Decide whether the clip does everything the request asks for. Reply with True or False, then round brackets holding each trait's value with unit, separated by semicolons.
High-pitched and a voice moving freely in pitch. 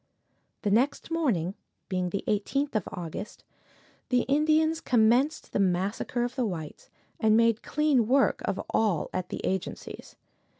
True (225 Hz; 6.3 semitones)